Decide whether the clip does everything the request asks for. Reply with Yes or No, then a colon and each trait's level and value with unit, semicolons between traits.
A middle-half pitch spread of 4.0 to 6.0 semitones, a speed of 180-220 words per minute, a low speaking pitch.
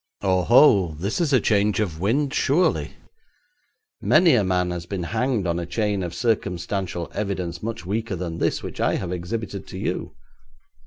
No: average, 4.3 semitones; average, 165 wpm; low, 100 Hz